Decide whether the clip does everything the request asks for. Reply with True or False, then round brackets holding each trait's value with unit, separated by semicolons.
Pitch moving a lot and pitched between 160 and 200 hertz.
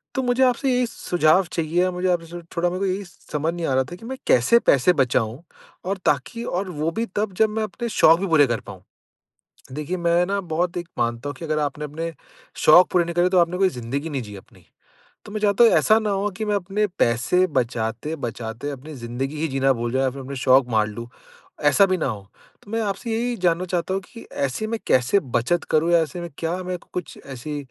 True (6.2 semitones; 165 Hz)